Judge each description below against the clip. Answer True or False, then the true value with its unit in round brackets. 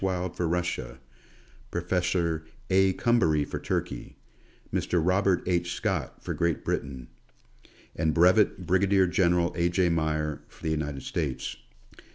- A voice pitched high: False (85 Hz)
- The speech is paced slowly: True (130 wpm)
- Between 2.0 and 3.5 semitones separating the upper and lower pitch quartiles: True (2.8 semitones)